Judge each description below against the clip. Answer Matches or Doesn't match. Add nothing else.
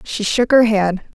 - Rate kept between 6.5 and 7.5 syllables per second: Doesn't match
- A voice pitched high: Matches